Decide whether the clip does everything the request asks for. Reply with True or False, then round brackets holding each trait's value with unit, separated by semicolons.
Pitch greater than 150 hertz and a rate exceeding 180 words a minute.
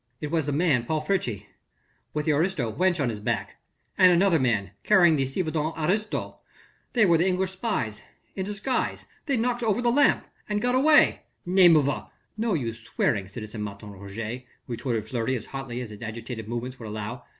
False (145 Hz; 190 wpm)